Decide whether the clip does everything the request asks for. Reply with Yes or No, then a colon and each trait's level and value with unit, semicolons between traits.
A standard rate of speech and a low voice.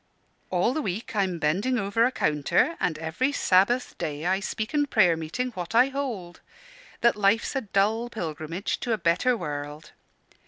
No: average, 165 wpm; high, 200 Hz